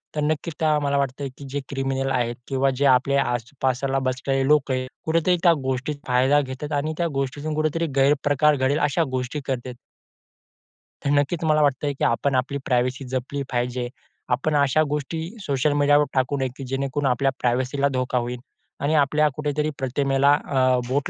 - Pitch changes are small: Yes, narrow, 2.0 semitones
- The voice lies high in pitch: No, medium, 140 Hz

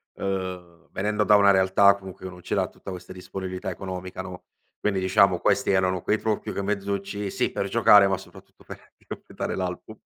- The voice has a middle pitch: No, very low, 95 Hz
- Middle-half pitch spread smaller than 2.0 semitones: Yes, narrow, 1.3 semitones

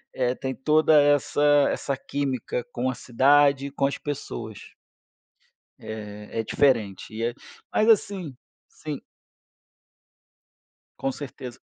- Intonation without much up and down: No, average, 3.1 semitones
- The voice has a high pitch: No, low, 135 Hz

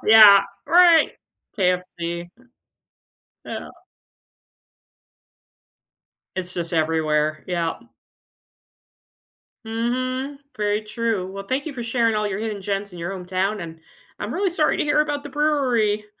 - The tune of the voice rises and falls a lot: Yes, wide, 6.0 semitones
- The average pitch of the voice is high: Yes, high, 210 Hz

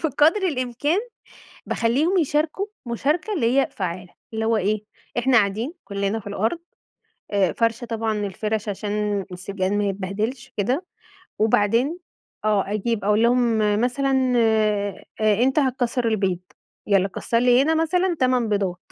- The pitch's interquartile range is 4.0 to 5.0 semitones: Yes, average, 4.3 semitones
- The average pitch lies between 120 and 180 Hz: No, high, 225 Hz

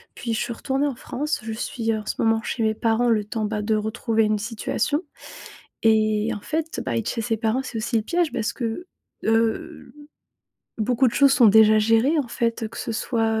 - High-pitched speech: Yes, high, 225 Hz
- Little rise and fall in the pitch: Yes, narrow, 2.2 semitones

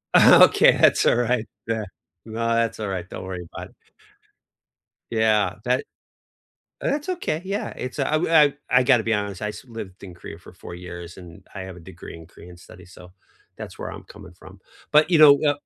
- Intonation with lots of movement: Yes, wide, 5.8 semitones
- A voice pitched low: Yes, low, 105 Hz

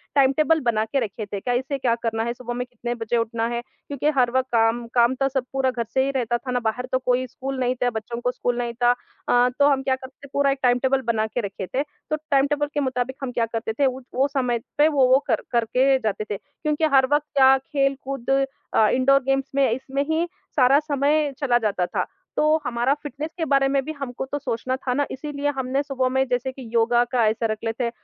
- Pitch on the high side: Yes, very high, 260 Hz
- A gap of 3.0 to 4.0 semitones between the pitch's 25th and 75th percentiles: No, narrow, 2.4 semitones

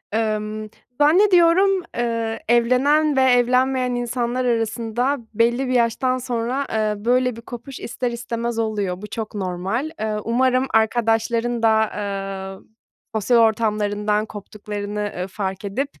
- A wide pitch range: No, average, 3.0 semitones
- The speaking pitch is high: Yes, high, 230 Hz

